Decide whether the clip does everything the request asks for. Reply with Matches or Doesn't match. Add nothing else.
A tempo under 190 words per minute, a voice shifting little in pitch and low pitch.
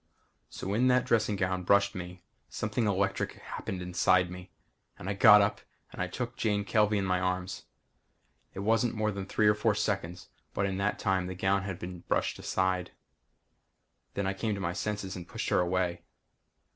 Matches